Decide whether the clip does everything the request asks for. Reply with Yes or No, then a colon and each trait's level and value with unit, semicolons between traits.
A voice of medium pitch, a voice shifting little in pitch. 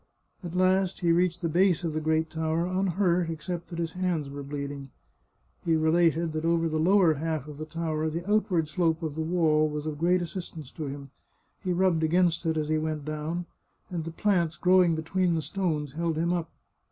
Yes: medium, 165 Hz; narrow, 2.2 semitones